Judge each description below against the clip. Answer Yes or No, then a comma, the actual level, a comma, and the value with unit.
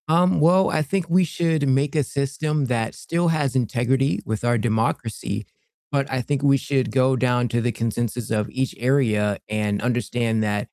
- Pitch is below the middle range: Yes, low, 130 Hz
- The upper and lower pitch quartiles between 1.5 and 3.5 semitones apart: No, average, 3.9 semitones